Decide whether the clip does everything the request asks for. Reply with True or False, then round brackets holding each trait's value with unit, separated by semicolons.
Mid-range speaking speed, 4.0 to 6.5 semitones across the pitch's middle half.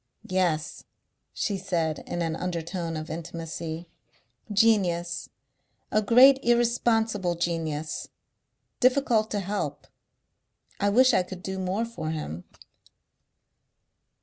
False (100 wpm; 4.9 semitones)